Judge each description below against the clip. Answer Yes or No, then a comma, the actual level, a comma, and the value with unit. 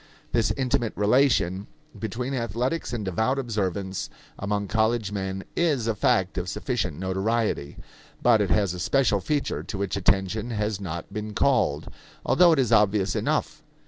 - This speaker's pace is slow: No, average, 150 wpm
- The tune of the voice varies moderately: Yes, average, 3.8 semitones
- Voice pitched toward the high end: No, low, 105 Hz